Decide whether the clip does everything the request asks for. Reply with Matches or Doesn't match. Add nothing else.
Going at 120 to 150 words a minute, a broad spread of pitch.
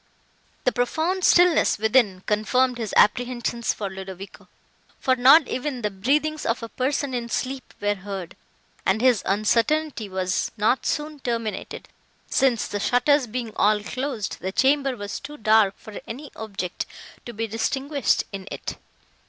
Doesn't match